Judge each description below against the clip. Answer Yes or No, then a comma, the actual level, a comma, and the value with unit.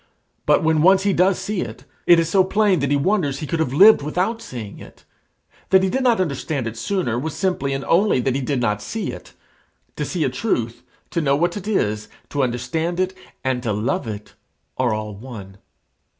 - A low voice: No, medium, 150 Hz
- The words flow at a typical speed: No, fast, 210 wpm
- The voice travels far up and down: Yes, wide, 7.3 semitones